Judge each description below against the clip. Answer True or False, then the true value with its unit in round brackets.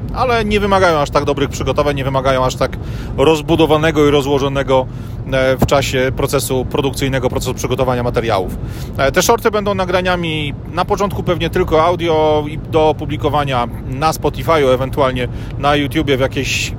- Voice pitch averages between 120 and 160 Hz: True (140 Hz)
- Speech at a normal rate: True (145 wpm)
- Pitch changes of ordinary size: True (3.6 semitones)